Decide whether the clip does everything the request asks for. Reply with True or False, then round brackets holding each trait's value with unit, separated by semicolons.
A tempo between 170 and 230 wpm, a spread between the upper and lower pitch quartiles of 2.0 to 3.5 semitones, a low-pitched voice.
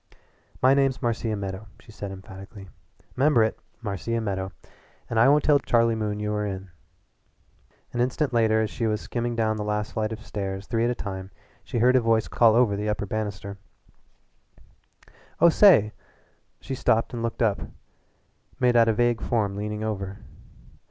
True (175 wpm; 2.6 semitones; 110 Hz)